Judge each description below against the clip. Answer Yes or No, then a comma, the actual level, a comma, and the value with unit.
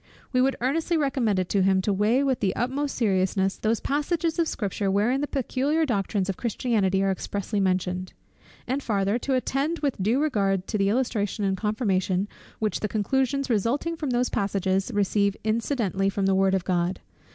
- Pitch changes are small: No, average, 5.3 semitones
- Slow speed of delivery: No, average, 180 wpm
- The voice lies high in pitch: Yes, high, 210 Hz